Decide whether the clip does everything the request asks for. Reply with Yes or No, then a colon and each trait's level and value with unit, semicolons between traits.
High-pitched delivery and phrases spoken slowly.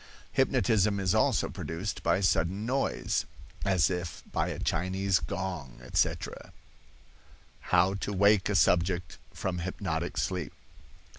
No: very low, 95 Hz; slow, 120 wpm